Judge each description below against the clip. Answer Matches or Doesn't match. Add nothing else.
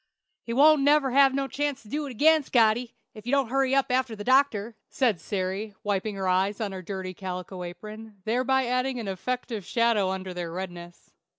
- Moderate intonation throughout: Doesn't match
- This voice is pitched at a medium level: Doesn't match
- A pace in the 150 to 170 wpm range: Doesn't match